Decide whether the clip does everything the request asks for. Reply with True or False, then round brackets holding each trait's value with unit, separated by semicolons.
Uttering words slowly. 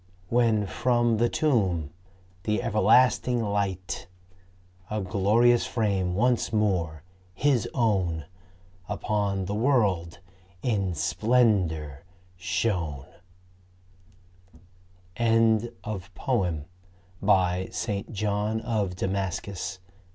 True (70 wpm)